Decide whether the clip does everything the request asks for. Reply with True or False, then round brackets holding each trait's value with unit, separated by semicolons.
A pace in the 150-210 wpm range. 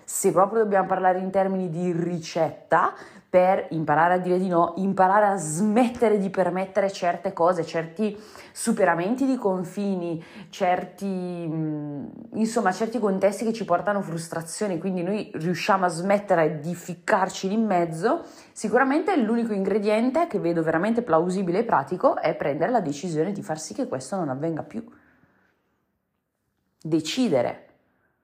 False (140 wpm)